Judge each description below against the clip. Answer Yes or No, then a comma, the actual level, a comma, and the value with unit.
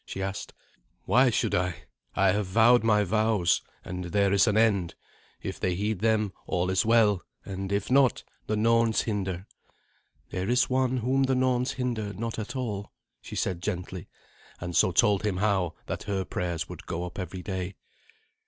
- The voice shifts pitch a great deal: No, average, 3.6 semitones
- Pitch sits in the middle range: No, low, 100 Hz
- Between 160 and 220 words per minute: Yes, average, 175 wpm